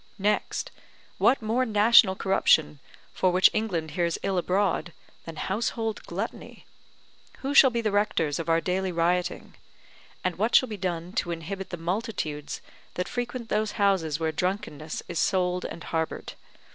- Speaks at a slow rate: No, average, 150 wpm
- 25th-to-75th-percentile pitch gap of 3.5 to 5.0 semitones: Yes, average, 4.1 semitones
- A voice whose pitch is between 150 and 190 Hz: Yes, medium, 185 Hz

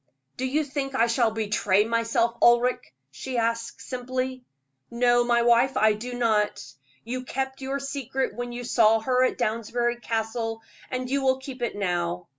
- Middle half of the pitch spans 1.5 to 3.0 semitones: Yes, narrow, 2.4 semitones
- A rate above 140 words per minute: Yes, average, 165 wpm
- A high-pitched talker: Yes, high, 240 Hz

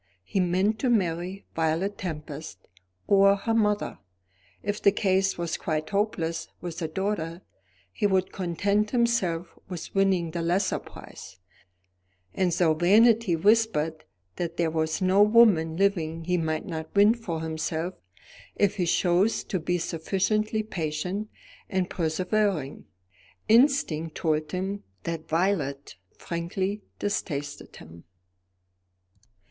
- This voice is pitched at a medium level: Yes, medium, 180 Hz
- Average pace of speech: No, slow, 120 wpm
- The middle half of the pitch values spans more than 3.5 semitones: Yes, average, 4.0 semitones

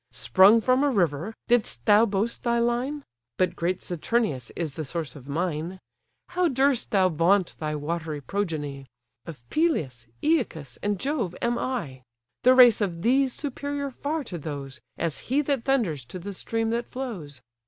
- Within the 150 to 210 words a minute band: Yes, average, 165 wpm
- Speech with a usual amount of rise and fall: No, wide, 8.3 semitones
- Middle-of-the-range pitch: No, high, 200 Hz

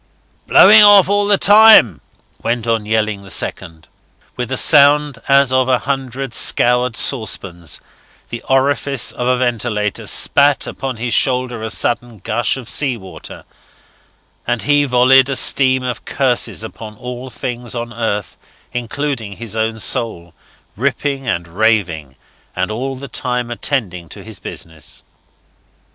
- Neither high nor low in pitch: No, low, 120 Hz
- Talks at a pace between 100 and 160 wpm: Yes, average, 140 wpm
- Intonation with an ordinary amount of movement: Yes, average, 3.5 semitones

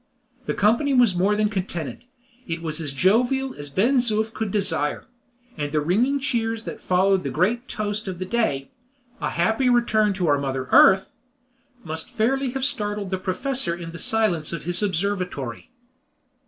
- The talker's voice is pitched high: Yes, high, 195 Hz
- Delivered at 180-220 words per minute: No, average, 170 wpm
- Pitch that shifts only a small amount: No, average, 5.1 semitones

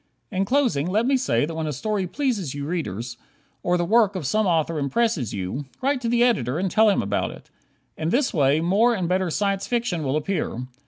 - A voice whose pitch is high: No, medium, 180 Hz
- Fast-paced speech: Yes, fast, 215 wpm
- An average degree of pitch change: No, wide, 7.2 semitones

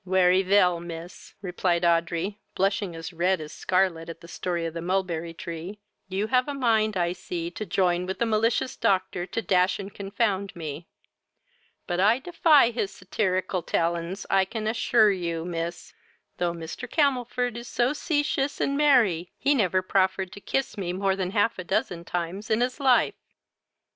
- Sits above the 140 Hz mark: Yes, high, 190 Hz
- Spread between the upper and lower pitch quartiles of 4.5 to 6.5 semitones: No, average, 4.1 semitones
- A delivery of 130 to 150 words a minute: No, average, 170 wpm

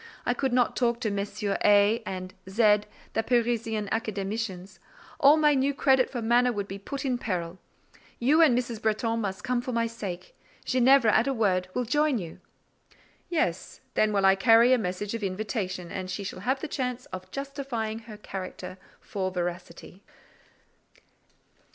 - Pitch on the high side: Yes, high, 220 Hz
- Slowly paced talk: No, average, 165 wpm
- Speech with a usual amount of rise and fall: Yes, average, 4.4 semitones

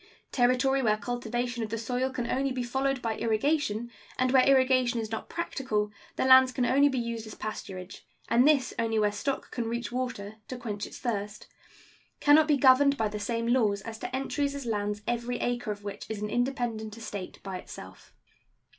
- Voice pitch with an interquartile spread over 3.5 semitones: No, average, 3.2 semitones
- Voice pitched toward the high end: Yes, high, 240 Hz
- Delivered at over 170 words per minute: Yes, average, 195 wpm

